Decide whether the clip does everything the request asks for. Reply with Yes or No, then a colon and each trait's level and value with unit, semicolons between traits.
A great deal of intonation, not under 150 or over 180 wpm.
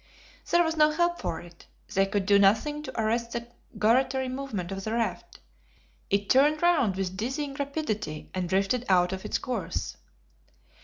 Yes: wide, 6.4 semitones; average, 165 wpm